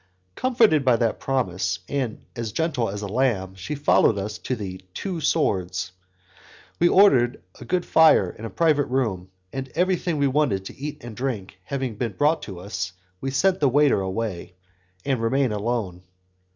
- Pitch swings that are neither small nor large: No, wide, 6.5 semitones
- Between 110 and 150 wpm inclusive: No, average, 170 wpm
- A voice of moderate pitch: No, low, 125 Hz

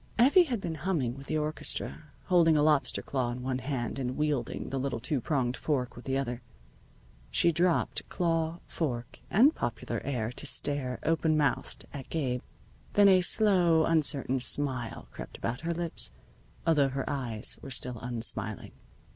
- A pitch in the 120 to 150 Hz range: Yes, medium, 140 Hz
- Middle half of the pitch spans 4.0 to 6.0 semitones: Yes, average, 4.7 semitones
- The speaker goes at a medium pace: Yes, average, 165 wpm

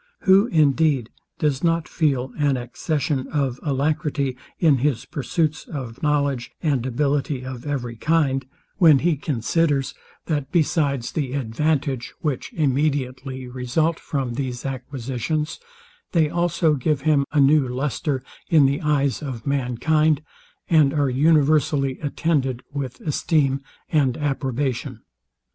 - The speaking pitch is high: No, medium, 140 Hz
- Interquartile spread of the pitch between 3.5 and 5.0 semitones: No, average, 2.8 semitones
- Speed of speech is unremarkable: No, slow, 120 wpm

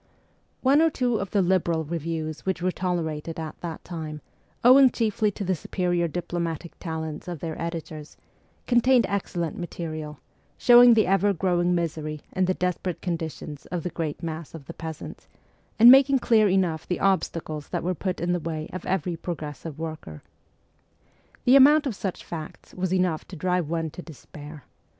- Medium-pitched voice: Yes, medium, 175 Hz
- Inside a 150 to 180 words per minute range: Yes, average, 175 wpm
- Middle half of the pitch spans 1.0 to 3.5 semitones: Yes, average, 3.1 semitones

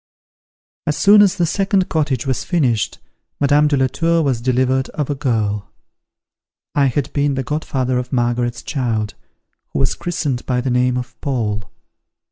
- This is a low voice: Yes, low, 130 Hz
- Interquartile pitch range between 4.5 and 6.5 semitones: No, average, 3.3 semitones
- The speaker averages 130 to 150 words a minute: No, average, 160 wpm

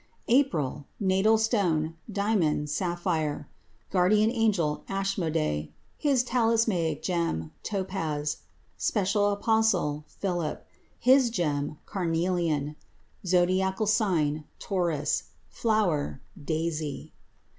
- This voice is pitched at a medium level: Yes, medium, 180 Hz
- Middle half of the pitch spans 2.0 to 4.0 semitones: No, wide, 5.5 semitones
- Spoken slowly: Yes, slow, 80 wpm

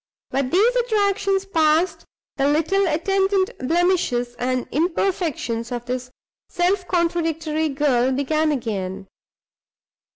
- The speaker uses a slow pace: Yes, slow, 100 wpm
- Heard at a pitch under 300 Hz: No, very high, 315 Hz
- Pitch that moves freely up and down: Yes, wide, 6.5 semitones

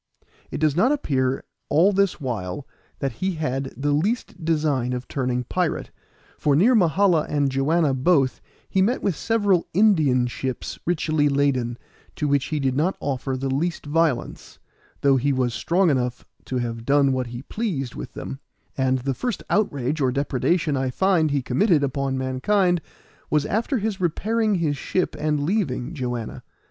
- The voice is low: No, medium, 145 Hz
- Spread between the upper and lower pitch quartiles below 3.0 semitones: No, average, 5.2 semitones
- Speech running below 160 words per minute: No, average, 165 wpm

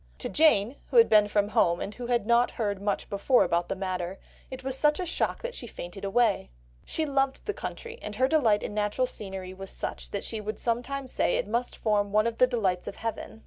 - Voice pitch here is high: Yes, high, 220 Hz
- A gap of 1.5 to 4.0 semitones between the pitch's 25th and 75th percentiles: No, average, 4.4 semitones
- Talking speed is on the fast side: Yes, fast, 230 wpm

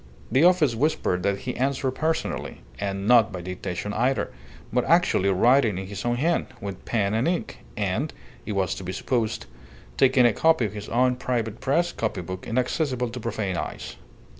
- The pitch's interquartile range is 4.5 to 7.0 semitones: Yes, average, 4.9 semitones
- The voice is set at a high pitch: No, low, 115 Hz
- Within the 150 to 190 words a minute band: Yes, average, 180 wpm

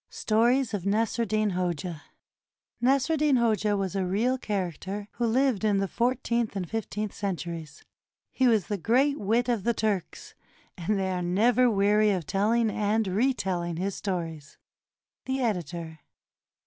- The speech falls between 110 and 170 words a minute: Yes, average, 150 wpm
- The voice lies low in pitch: No, high, 210 Hz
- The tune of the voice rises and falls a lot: No, average, 4.1 semitones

